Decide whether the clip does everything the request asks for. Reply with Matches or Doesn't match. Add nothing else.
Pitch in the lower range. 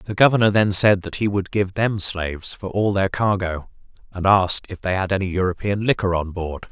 Matches